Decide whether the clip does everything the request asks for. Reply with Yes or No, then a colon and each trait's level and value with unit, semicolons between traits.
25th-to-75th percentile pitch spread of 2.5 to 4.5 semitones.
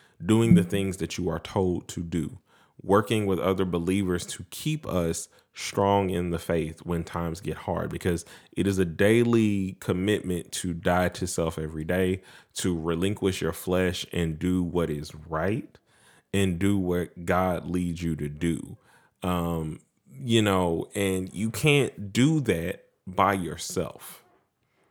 Yes: average, 2.8 semitones